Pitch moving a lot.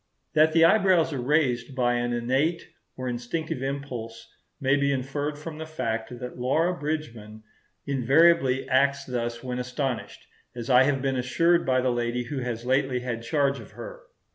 No: average, 3.6 semitones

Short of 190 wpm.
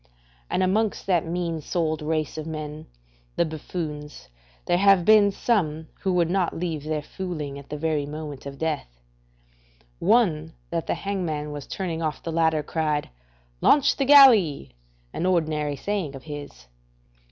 Yes: average, 155 wpm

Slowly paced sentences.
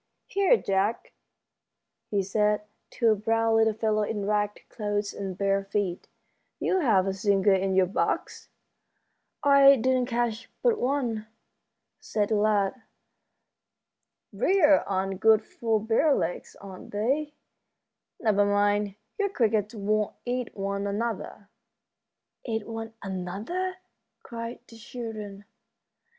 Yes: slow, 120 wpm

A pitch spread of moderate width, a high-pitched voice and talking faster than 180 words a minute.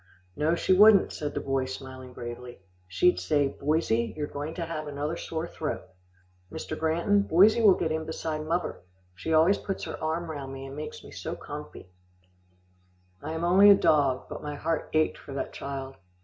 No: average, 3.4 semitones; medium, 155 Hz; average, 190 wpm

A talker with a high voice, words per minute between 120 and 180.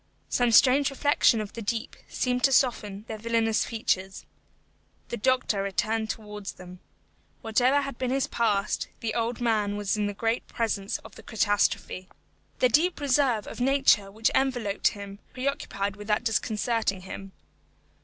Yes: high, 225 Hz; average, 150 wpm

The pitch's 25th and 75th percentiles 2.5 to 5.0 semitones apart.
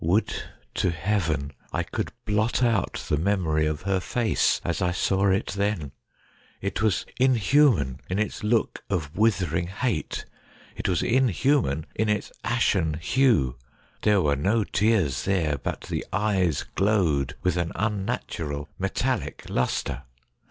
No: wide, 5.5 semitones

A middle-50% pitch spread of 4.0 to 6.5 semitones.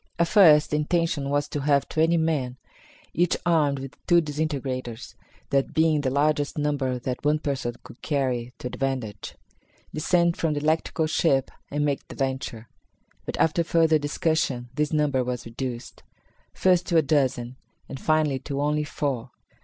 No: average, 3.1 semitones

